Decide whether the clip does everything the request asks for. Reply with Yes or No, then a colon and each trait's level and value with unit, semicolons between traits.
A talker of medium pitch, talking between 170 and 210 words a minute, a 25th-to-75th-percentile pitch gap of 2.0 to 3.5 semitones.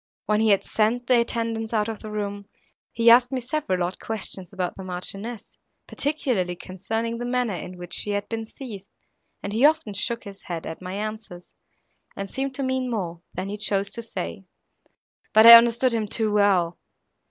No: high, 215 Hz; average, 185 wpm; average, 3.1 semitones